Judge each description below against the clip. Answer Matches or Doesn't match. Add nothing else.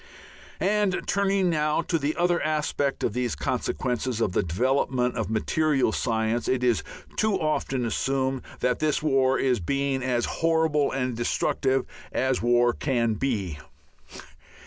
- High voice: Doesn't match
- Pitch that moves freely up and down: Doesn't match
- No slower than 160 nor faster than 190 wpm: Doesn't match